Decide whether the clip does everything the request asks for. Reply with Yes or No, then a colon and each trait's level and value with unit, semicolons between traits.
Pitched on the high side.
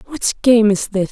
Yes: high, 220 Hz